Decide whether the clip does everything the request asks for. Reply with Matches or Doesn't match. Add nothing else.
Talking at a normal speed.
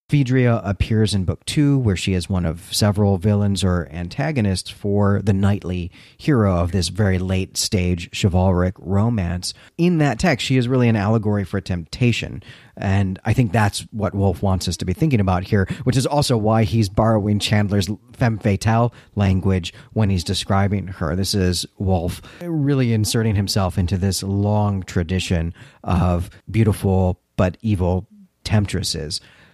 Matches